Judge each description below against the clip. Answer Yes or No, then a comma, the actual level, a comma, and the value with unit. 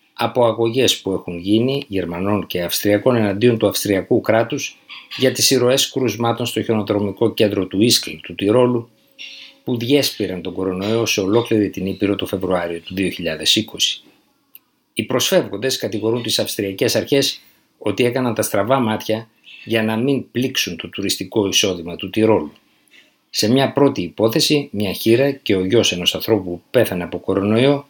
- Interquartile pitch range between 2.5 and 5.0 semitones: Yes, average, 4.4 semitones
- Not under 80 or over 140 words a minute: No, average, 150 wpm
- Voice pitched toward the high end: No, low, 110 Hz